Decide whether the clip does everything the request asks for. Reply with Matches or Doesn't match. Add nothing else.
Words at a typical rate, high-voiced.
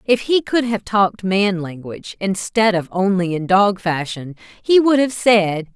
Matches